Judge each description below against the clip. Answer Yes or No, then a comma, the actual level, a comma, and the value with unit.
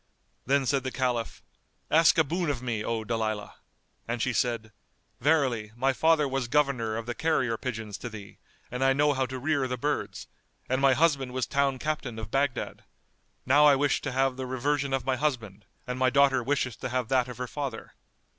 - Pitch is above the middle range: No, low, 130 Hz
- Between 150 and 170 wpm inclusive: No, average, 200 wpm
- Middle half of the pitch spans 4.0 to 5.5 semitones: No, average, 2.8 semitones